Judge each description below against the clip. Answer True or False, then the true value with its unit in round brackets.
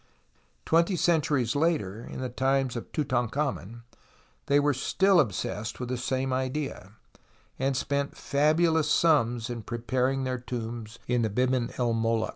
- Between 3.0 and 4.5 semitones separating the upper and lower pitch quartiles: True (3.4 semitones)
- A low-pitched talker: True (130 Hz)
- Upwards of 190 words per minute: False (140 wpm)